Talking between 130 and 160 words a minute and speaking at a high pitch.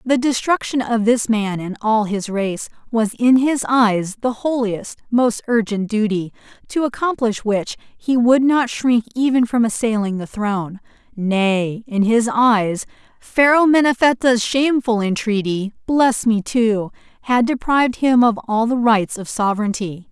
Yes: average, 145 wpm; high, 230 Hz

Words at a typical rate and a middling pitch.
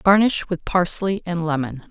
Yes: average, 160 wpm; medium, 175 Hz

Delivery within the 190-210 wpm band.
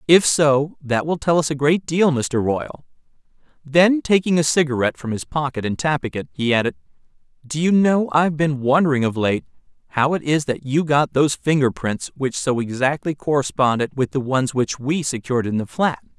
Yes: average, 195 wpm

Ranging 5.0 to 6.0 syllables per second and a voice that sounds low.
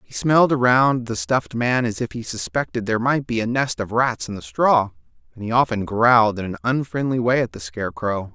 Yes: 5.5 syllables/s; low, 115 Hz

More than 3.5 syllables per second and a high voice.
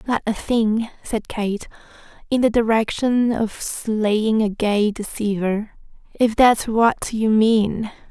No: 3.3 syllables/s; high, 220 Hz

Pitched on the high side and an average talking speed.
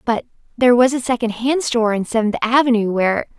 Yes: high, 235 Hz; average, 175 wpm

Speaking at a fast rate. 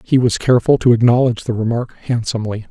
No: average, 175 wpm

